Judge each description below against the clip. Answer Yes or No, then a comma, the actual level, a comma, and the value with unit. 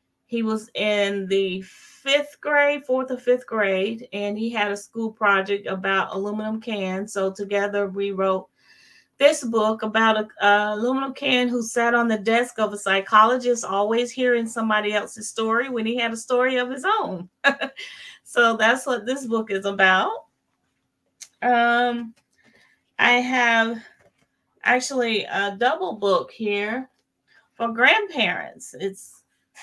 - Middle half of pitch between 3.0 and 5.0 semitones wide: Yes, average, 3.3 semitones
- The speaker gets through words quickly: No, average, 140 wpm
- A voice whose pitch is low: No, high, 225 Hz